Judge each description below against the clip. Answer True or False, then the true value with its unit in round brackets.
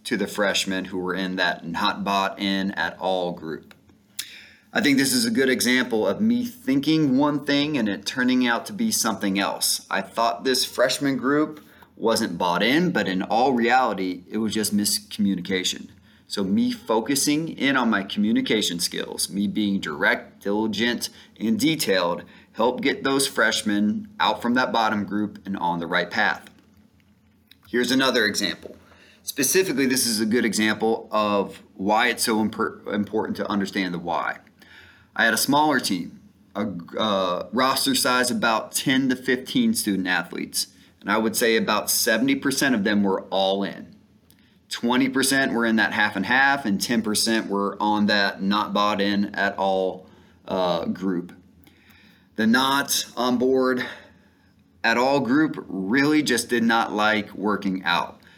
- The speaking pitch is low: True (110 Hz)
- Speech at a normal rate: True (160 wpm)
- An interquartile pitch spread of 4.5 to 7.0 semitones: True (5.2 semitones)